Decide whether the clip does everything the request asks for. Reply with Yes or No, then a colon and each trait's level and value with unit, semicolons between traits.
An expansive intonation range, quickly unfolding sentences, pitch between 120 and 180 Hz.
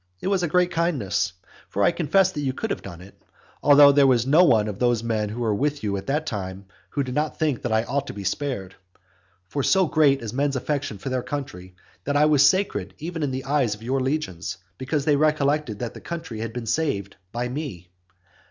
Yes: wide, 5.7 semitones; fast, 225 wpm; low, 135 Hz